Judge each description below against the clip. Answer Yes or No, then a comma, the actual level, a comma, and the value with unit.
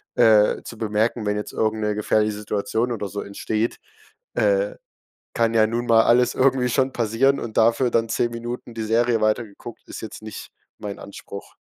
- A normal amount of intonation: No, narrow, 2.0 semitones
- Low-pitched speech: Yes, low, 115 Hz